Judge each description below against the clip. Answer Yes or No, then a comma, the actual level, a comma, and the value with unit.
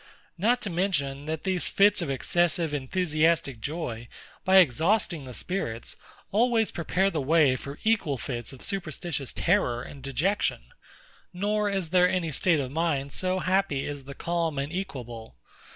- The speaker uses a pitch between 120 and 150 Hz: No, medium, 165 Hz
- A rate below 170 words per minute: Yes, average, 150 wpm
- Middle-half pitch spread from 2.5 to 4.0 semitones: No, wide, 5.4 semitones